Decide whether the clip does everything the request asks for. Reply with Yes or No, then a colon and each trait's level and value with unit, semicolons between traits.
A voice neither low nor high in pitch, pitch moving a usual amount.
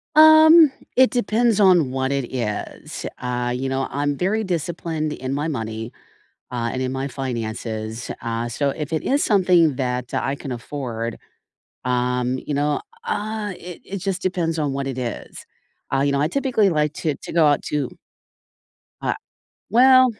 No: medium, 145 Hz; wide, 6.6 semitones